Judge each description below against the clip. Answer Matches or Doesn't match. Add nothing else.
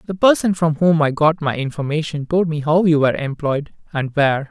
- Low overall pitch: Doesn't match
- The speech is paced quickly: Matches